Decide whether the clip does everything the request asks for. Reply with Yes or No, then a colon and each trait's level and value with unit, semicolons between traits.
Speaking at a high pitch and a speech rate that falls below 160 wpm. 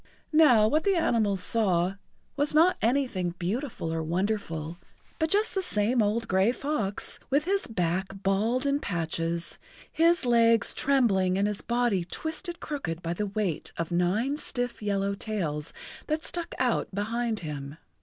Yes: high, 215 Hz; average, 150 wpm